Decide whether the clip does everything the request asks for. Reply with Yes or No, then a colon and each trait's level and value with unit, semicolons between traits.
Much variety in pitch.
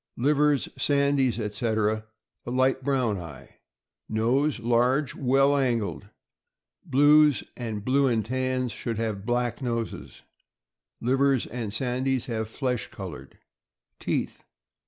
No: average, 3.4 semitones